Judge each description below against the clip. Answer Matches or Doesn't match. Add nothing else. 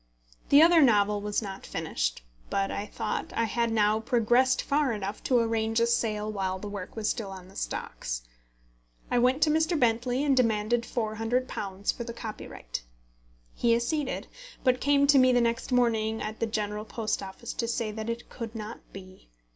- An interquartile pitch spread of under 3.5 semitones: Matches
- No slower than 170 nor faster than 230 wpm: Matches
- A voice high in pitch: Matches